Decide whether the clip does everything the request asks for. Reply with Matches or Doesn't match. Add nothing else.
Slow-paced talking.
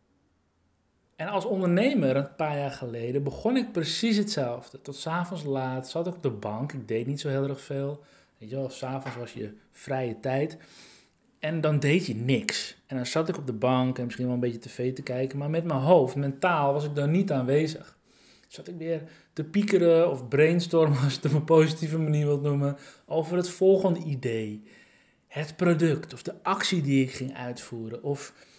Doesn't match